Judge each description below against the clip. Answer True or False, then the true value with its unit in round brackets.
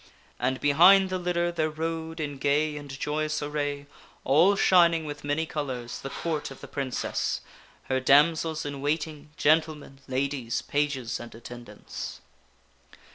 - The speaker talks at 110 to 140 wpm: True (135 wpm)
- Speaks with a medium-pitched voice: True (145 Hz)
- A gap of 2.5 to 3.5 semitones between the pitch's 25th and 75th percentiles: True (2.8 semitones)